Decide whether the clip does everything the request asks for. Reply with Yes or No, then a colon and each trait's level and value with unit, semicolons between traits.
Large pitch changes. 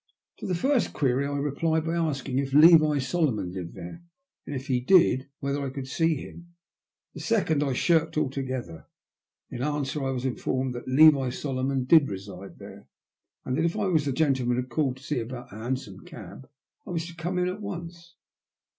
No: average, 4.1 semitones